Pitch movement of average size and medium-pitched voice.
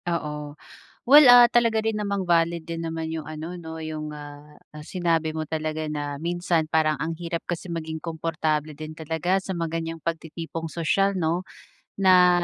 No: narrow, 1.9 semitones; medium, 165 Hz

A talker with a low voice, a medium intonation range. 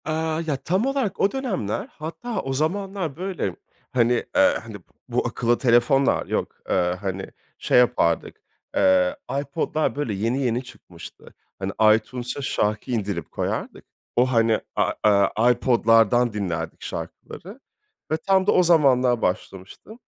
No: low, 125 Hz; wide, 7.2 semitones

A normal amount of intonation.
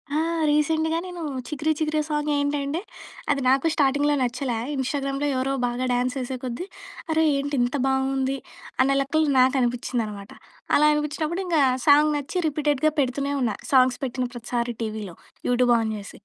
Yes: average, 3.2 semitones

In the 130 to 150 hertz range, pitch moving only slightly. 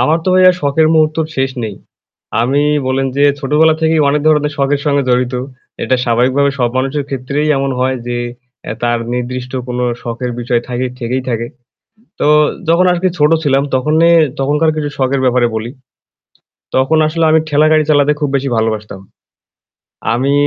No: low, 135 Hz; average, 3.3 semitones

